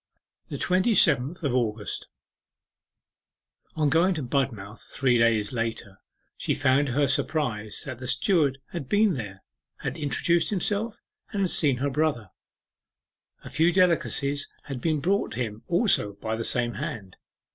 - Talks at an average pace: Yes, average, 145 wpm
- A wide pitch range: Yes, wide, 6.2 semitones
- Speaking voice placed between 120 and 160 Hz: Yes, medium, 140 Hz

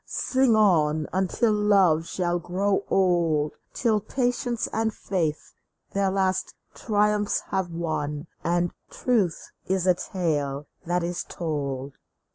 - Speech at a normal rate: No, slow, 115 wpm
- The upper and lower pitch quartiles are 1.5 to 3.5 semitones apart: No, average, 4.3 semitones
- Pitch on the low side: No, medium, 180 Hz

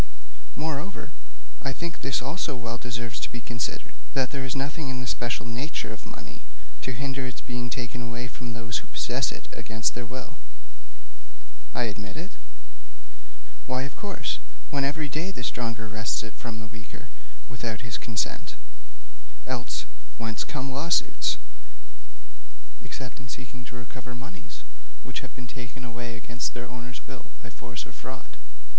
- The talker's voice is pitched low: Yes, low, 125 Hz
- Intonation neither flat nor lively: No, narrow, 2.2 semitones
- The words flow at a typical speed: Yes, average, 160 wpm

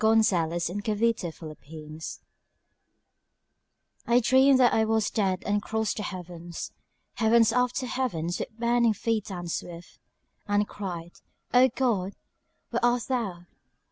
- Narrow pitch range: No, average, 5.1 semitones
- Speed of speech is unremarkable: No, slow, 130 wpm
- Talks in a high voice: Yes, high, 215 Hz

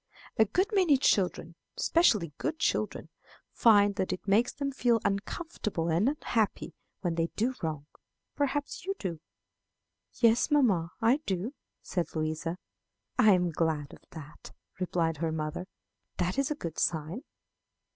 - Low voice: No, high, 195 Hz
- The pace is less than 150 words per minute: Yes, average, 140 wpm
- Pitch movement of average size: No, wide, 7.3 semitones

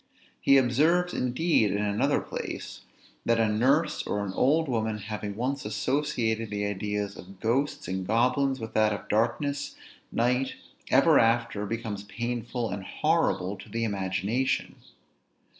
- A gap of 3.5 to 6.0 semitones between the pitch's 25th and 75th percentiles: Yes, average, 4.2 semitones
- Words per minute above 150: No, average, 140 wpm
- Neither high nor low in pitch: No, low, 115 Hz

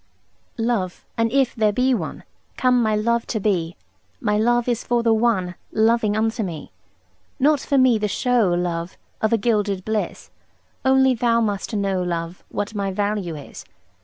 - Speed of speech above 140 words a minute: Yes, average, 165 wpm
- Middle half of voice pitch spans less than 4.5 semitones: Yes, average, 3.4 semitones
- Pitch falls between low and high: No, high, 220 Hz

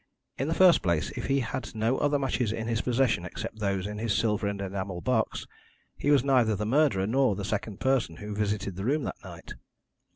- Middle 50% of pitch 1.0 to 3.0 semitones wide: No, average, 4.7 semitones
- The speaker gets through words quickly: Yes, fast, 215 wpm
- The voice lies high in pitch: No, low, 110 Hz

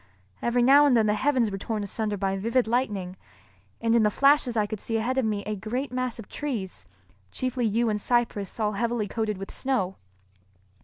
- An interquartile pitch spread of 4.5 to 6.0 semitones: No, average, 3.2 semitones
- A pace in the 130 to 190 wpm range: No, average, 200 wpm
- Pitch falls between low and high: No, high, 225 Hz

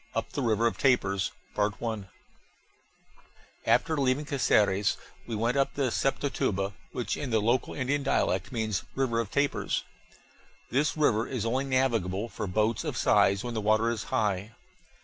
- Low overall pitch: Yes, low, 115 Hz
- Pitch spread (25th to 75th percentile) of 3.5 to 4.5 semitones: Yes, average, 4.1 semitones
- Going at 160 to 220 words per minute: No, average, 150 wpm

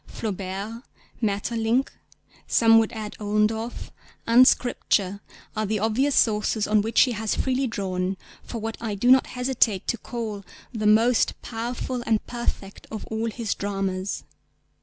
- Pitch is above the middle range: Yes, high, 220 Hz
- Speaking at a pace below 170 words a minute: Yes, average, 140 wpm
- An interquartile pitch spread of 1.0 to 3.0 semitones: Yes, narrow, 2.4 semitones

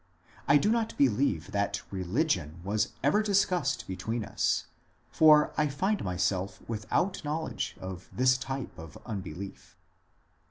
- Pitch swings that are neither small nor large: No, wide, 8.2 semitones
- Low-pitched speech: Yes, low, 115 Hz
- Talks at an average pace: No, slow, 125 wpm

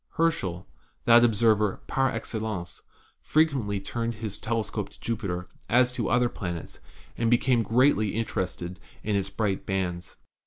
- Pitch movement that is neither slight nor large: Yes, average, 3.6 semitones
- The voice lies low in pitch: Yes, low, 110 Hz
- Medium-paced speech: No, slow, 130 wpm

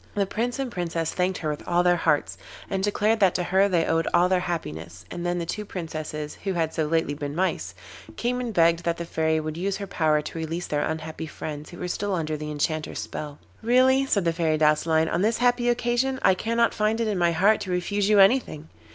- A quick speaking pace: Yes, fast, 230 wpm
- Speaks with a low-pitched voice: No, medium, 175 Hz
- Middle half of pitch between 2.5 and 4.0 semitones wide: No, average, 4.4 semitones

